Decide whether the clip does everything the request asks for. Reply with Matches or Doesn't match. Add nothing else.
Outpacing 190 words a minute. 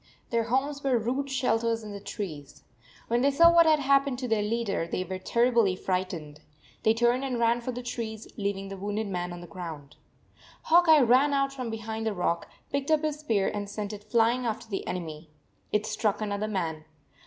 Matches